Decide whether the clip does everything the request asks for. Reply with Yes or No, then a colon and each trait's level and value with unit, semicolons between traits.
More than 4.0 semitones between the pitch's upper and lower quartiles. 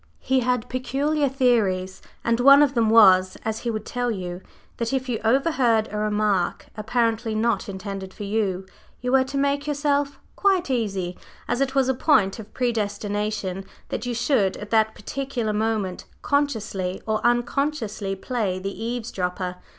Yes: average, 4.4 semitones